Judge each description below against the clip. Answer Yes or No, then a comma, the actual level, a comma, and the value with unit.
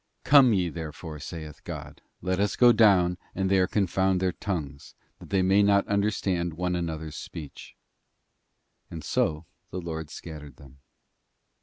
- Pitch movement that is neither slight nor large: Yes, average, 3.5 semitones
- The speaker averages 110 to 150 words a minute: Yes, average, 145 wpm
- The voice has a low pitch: Yes, very low, 90 Hz